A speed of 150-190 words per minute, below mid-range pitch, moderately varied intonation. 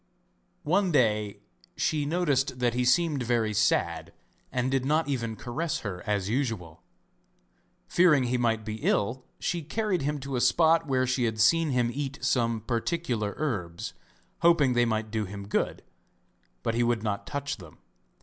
Yes: average, 160 wpm; low, 125 Hz; average, 4.9 semitones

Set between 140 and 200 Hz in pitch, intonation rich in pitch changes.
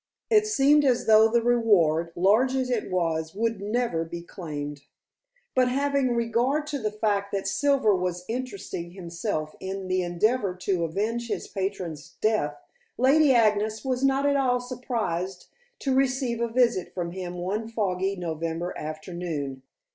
No: high, 210 Hz; wide, 5.9 semitones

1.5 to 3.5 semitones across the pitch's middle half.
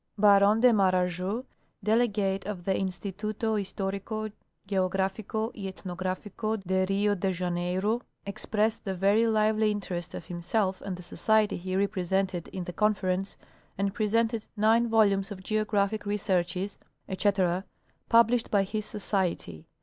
Yes: narrow, 2.5 semitones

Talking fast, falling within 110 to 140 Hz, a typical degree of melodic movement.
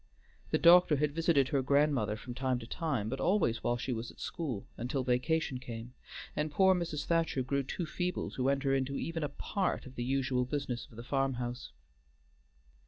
No: average, 185 wpm; low, 135 Hz; average, 3.8 semitones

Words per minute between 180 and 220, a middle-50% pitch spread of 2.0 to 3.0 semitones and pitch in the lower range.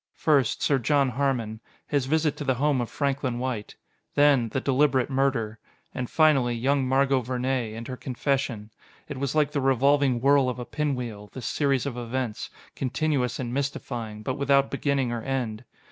No: average, 170 wpm; narrow, 2.5 semitones; low, 130 Hz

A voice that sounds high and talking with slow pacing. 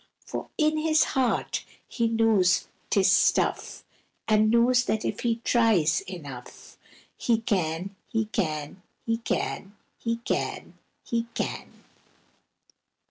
Yes: high, 220 Hz; slow, 115 wpm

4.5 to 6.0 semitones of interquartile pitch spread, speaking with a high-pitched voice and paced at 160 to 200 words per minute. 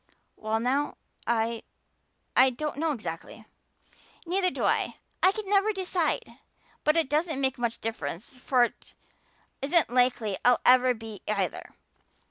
No: wide, 5.6 semitones; very high, 255 Hz; average, 140 wpm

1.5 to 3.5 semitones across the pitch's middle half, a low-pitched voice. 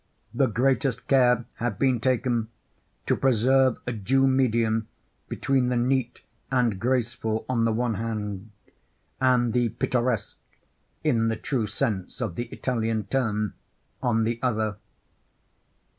Yes: narrow, 2.5 semitones; low, 120 Hz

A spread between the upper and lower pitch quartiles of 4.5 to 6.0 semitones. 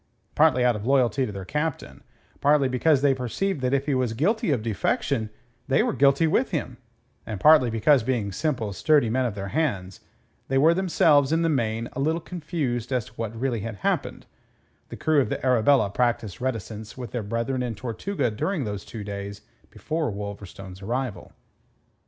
Yes: average, 4.8 semitones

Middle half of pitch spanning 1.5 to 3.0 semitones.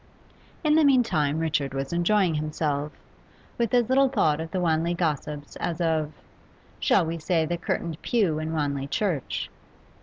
No: average, 3.4 semitones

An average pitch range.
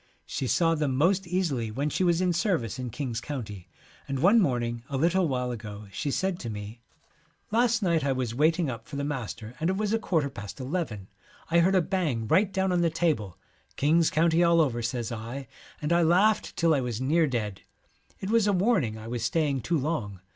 No: wide, 6.5 semitones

